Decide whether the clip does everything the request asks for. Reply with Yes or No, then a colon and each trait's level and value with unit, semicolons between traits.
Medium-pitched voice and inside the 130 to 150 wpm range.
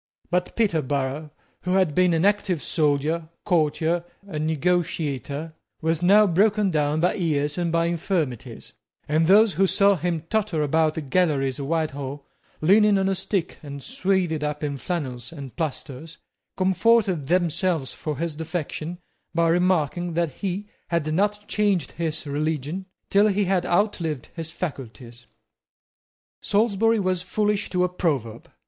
Yes: medium, 165 Hz; average, 140 wpm